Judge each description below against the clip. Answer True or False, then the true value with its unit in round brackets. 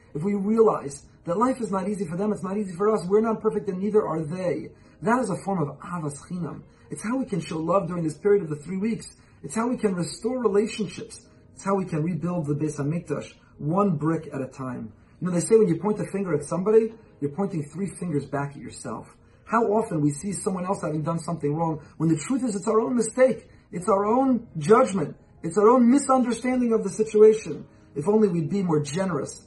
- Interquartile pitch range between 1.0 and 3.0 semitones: False (5.6 semitones)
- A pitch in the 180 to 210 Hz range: True (190 Hz)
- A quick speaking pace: True (230 wpm)